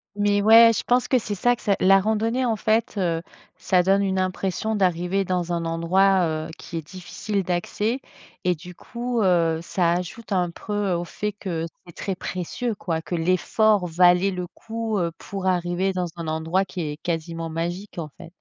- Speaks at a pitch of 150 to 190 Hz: Yes, medium, 185 Hz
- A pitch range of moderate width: Yes, average, 3.2 semitones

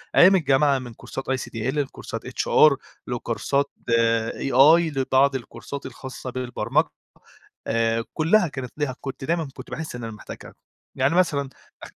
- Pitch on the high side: No, low, 135 Hz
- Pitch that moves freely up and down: No, average, 2.9 semitones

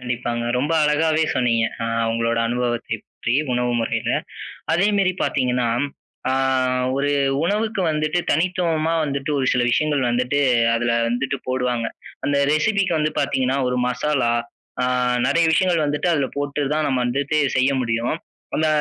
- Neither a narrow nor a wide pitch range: Yes, average, 4.0 semitones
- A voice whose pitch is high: No, medium, 140 Hz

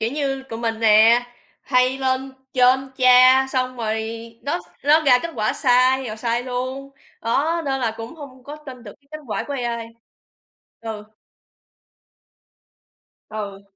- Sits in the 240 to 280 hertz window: Yes, very high, 255 Hz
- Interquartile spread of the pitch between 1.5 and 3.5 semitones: Yes, average, 2.7 semitones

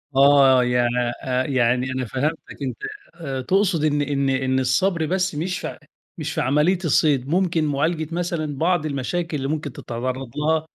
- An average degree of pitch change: Yes, average, 3.8 semitones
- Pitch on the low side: No, medium, 145 Hz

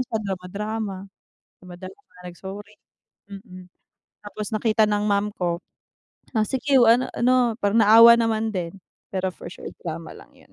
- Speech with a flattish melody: No, average, 3.2 semitones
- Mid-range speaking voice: No, high, 205 Hz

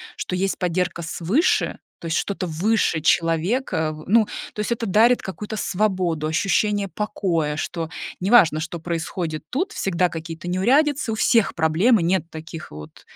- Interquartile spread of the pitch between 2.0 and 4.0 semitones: No, average, 4.6 semitones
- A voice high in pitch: No, medium, 180 Hz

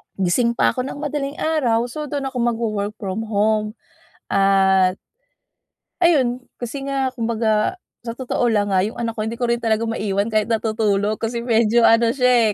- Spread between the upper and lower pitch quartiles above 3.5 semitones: No, narrow, 2.6 semitones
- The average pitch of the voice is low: No, high, 230 Hz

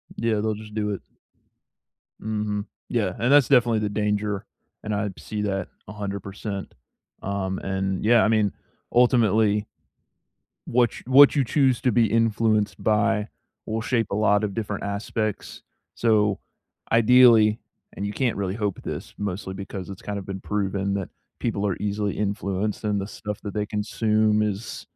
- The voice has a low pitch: Yes, low, 105 Hz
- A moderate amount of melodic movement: No, narrow, 1.9 semitones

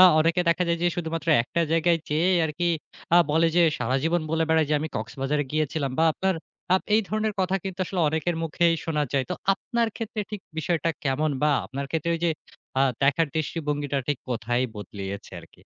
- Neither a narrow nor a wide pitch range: Yes, average, 3.3 semitones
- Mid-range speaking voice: Yes, medium, 160 Hz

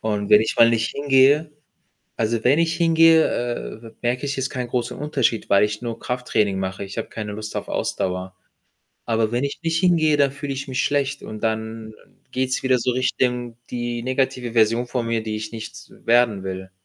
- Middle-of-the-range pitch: No, low, 120 Hz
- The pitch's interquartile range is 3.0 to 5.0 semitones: Yes, average, 3.5 semitones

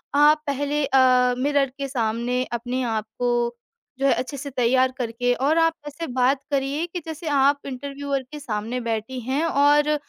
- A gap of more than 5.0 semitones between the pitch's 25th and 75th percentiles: No, narrow, 2.5 semitones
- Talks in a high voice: Yes, very high, 270 Hz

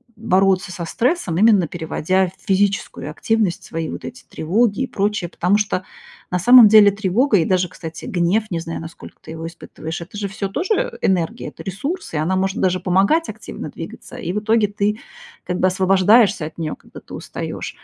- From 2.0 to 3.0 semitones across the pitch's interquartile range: No, average, 3.4 semitones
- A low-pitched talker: No, high, 190 Hz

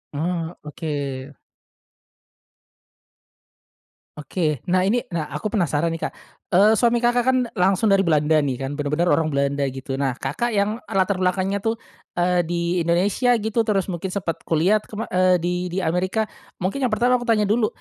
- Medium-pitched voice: Yes, medium, 180 Hz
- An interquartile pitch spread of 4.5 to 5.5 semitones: Yes, average, 5.1 semitones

